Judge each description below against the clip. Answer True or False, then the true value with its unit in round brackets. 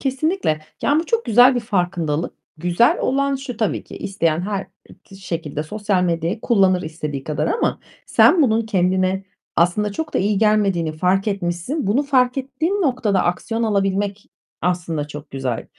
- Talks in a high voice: True (195 Hz)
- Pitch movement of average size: False (6.0 semitones)